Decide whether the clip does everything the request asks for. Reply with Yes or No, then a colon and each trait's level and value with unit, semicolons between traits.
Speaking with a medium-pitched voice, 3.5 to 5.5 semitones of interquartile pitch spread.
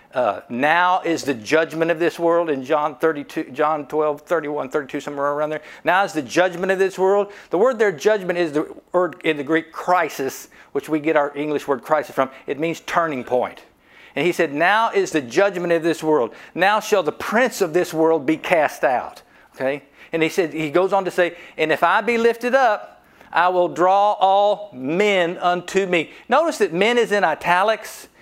Yes: medium, 170 Hz; average, 4.0 semitones